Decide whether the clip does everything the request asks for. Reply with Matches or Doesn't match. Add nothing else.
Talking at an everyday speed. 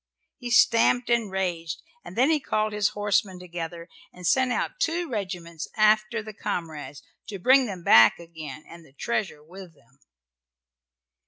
Matches